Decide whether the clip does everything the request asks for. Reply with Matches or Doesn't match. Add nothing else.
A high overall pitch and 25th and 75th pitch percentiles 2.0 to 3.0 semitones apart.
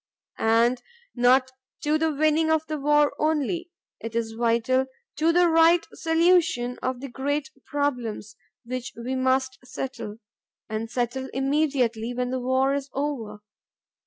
Doesn't match